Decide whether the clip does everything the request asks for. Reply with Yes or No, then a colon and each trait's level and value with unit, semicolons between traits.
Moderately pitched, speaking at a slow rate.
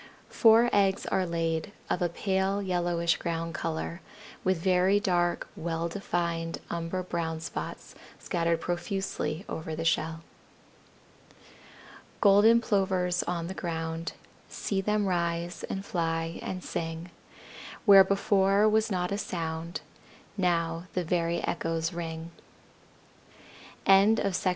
Yes: medium, 175 Hz; slow, 120 wpm